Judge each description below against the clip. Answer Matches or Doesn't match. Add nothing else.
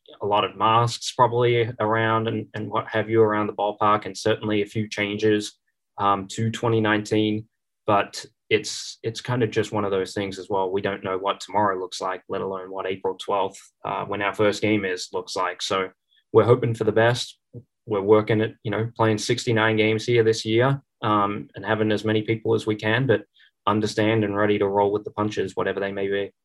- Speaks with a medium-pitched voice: Doesn't match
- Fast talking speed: Matches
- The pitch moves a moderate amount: Doesn't match